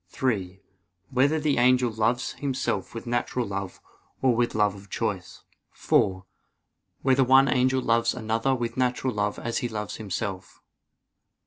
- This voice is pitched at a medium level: No, low, 120 Hz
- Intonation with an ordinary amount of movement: Yes, average, 3.6 semitones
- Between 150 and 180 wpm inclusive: No, average, 140 wpm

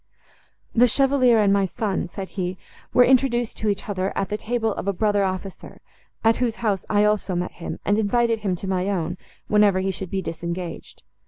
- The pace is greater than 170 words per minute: Yes, average, 195 wpm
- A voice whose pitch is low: No, high, 200 Hz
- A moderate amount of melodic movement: Yes, average, 3.1 semitones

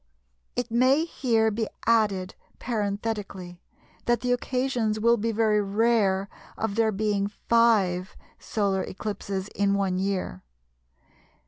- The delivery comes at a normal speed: No, slow, 115 wpm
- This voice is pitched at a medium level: No, high, 215 Hz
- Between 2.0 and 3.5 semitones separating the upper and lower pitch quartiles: Yes, average, 2.8 semitones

